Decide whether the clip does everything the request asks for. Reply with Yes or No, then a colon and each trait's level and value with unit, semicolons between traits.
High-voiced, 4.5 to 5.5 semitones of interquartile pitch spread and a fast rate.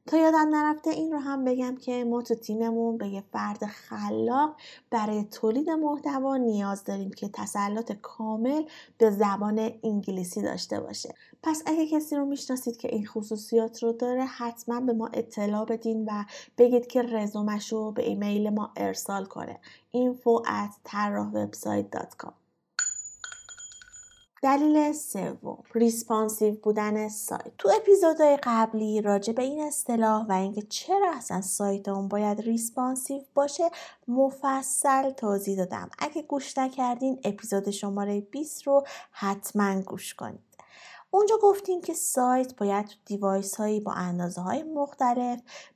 No: high, 230 Hz; average, 5.1 semitones; average, 130 wpm